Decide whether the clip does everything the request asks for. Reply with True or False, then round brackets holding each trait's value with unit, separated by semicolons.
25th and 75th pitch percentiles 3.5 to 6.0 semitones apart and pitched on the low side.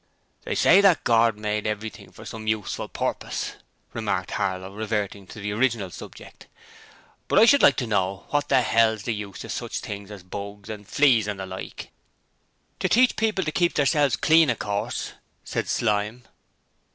True (4.6 semitones; 110 Hz)